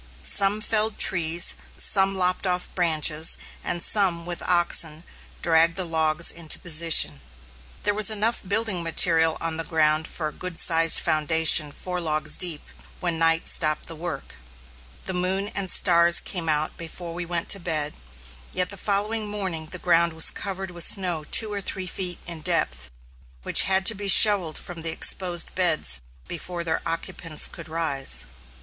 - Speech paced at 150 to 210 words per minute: Yes, average, 165 wpm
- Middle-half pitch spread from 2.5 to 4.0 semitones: Yes, average, 2.8 semitones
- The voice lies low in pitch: No, medium, 170 Hz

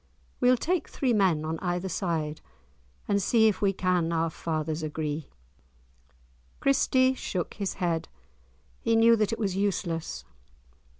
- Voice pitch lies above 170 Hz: Yes, medium, 185 Hz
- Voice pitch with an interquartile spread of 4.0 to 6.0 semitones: Yes, average, 5.3 semitones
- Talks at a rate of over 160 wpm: No, slow, 135 wpm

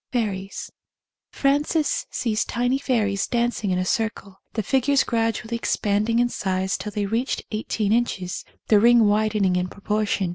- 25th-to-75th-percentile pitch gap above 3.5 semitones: No, average, 3.2 semitones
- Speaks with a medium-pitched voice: No, high, 215 Hz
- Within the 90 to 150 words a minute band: Yes, average, 145 wpm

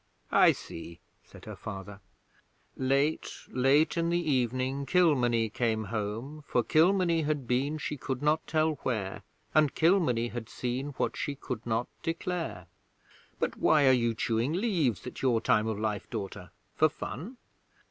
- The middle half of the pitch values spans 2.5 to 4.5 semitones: No, wide, 5.4 semitones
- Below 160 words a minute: Yes, average, 150 wpm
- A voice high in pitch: No, low, 130 Hz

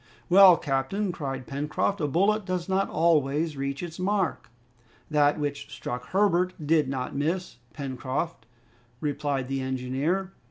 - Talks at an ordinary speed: No, slow, 130 wpm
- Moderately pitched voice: Yes, medium, 150 Hz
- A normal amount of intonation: Yes, average, 5.0 semitones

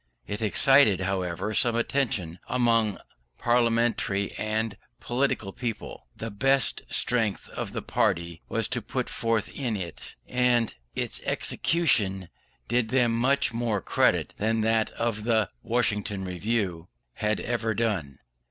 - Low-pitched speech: Yes, low, 110 Hz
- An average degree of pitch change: Yes, average, 3.1 semitones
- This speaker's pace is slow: Yes, slow, 125 wpm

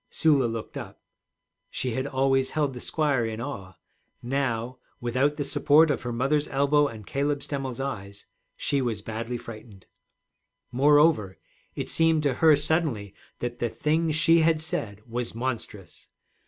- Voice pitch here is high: No, low, 130 Hz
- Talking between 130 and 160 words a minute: Yes, average, 150 wpm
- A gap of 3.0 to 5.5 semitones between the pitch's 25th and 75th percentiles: Yes, average, 4.2 semitones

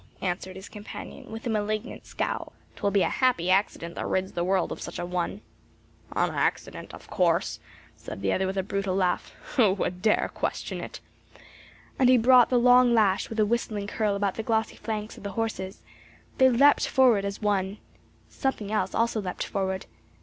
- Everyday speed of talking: Yes, average, 185 wpm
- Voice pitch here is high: Yes, high, 205 Hz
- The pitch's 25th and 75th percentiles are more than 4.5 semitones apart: No, average, 3.2 semitones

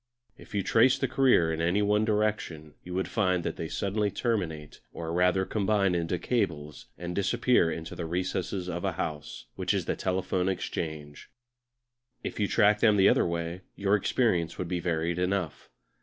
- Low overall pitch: Yes, very low, 90 Hz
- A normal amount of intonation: Yes, average, 3.5 semitones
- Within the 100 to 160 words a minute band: No, average, 170 wpm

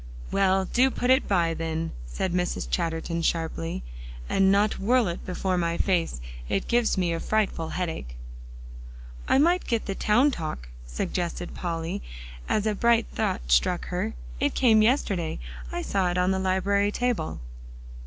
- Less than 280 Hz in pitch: Yes, medium, 185 Hz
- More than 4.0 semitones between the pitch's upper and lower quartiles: Yes, average, 4.4 semitones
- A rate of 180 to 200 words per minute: No, average, 155 wpm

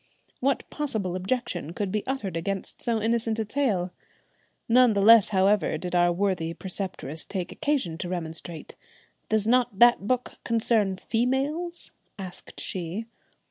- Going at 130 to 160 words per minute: Yes, average, 140 wpm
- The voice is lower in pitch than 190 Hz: No, high, 205 Hz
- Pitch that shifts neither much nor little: Yes, average, 4.8 semitones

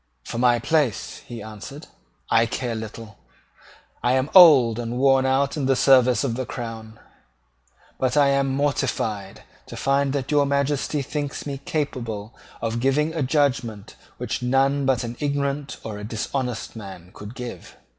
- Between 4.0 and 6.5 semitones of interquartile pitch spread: No, average, 3.4 semitones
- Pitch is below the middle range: Yes, low, 130 Hz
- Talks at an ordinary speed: Yes, average, 155 wpm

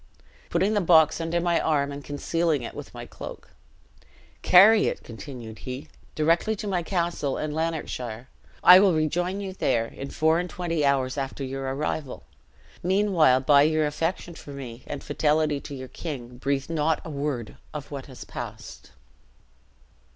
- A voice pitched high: No, medium, 150 Hz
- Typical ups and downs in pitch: Yes, average, 4.0 semitones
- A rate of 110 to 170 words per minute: Yes, average, 160 wpm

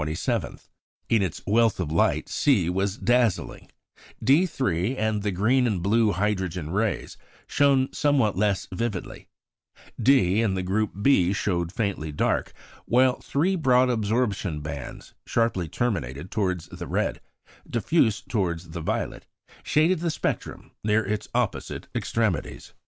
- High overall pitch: No, low, 105 Hz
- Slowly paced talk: Yes, slow, 130 wpm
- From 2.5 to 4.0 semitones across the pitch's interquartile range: No, average, 5.2 semitones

